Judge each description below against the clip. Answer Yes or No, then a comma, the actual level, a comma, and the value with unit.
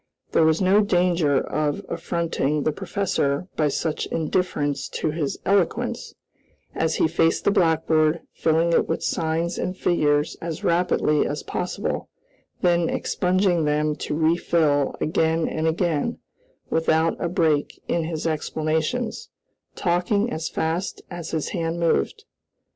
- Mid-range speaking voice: Yes, medium, 165 Hz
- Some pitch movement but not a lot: No, narrow, 2.1 semitones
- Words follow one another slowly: Yes, slow, 130 wpm